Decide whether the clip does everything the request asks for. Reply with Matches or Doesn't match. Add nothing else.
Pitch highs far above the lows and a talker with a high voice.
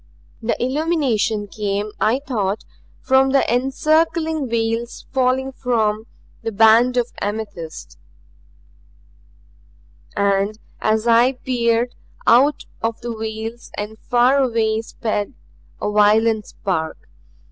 Doesn't match